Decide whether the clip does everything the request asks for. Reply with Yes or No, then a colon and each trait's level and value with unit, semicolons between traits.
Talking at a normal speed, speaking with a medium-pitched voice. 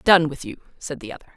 No: fast, 265 wpm; medium, 145 Hz